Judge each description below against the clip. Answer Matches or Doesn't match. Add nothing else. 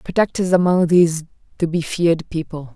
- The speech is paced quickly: Doesn't match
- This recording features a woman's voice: Matches